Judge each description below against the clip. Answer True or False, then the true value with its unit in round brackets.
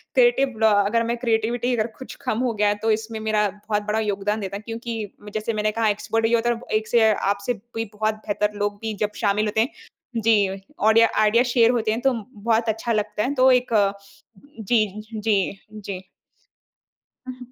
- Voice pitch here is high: True (220 Hz)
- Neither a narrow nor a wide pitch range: False (1.8 semitones)